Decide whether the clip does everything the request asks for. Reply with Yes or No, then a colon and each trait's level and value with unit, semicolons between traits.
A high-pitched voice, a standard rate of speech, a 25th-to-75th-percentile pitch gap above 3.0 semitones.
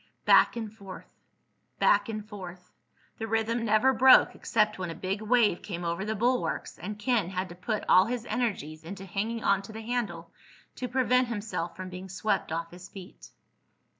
Yes: high, 205 Hz; average, 175 wpm; average, 3.8 semitones